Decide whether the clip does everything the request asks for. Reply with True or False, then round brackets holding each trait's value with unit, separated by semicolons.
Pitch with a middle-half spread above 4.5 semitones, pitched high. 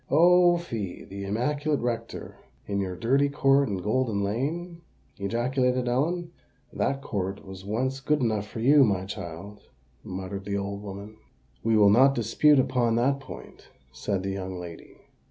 False (5.5 semitones; 115 Hz)